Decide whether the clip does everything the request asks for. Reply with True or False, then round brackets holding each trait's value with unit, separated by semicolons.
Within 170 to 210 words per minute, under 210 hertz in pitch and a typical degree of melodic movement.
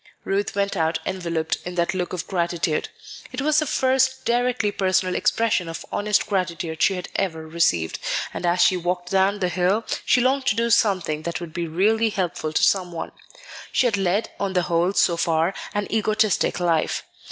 True (185 wpm; 185 Hz; 3.4 semitones)